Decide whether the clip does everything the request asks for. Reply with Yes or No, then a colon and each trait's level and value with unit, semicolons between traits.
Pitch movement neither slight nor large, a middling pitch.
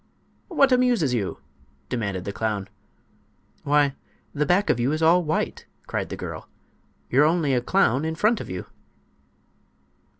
No: wide, 6.9 semitones; medium, 150 Hz